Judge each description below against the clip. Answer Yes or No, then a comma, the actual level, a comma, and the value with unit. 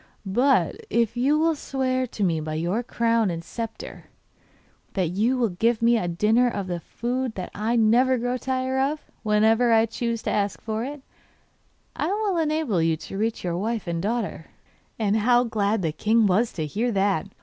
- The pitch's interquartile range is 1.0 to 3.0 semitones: No, average, 4.0 semitones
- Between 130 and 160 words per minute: No, average, 185 wpm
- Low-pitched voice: No, high, 225 Hz